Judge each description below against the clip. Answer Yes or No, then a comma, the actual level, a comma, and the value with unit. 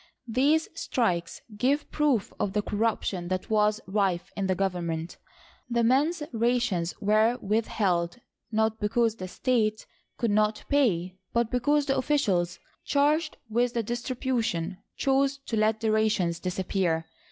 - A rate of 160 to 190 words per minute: No, slow, 135 wpm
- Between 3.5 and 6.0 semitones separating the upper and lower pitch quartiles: Yes, average, 4.7 semitones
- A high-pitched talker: Yes, high, 220 Hz